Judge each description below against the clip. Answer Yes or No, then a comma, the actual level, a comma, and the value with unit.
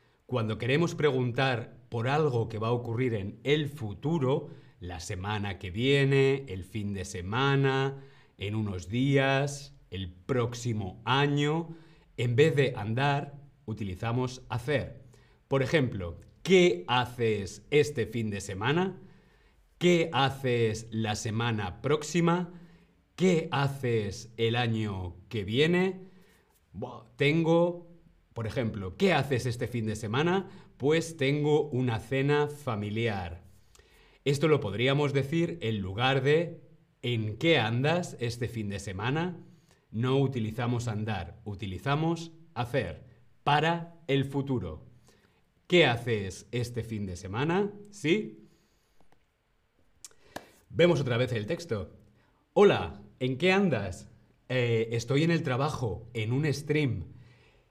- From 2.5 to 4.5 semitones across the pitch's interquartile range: No, average, 5.0 semitones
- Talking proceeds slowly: Yes, slow, 115 wpm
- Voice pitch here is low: Yes, low, 125 Hz